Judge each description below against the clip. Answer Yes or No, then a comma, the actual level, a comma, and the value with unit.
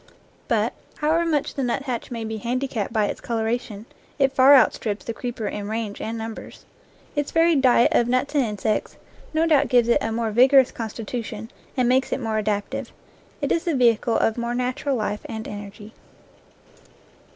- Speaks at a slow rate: No, average, 175 wpm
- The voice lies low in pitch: No, high, 235 Hz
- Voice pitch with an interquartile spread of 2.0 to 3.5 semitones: Yes, average, 3.2 semitones